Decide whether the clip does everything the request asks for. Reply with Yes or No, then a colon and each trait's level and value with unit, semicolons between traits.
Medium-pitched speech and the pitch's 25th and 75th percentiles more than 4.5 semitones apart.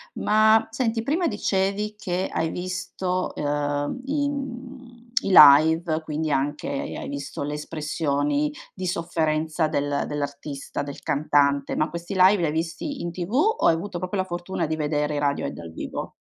Yes: medium, 165 Hz; average, 5.2 semitones